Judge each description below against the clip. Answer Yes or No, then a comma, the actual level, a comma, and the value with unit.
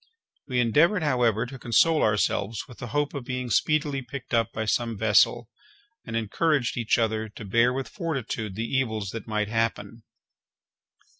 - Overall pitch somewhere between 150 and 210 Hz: No, low, 115 Hz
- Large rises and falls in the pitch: No, average, 3.3 semitones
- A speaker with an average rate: Yes, average, 160 wpm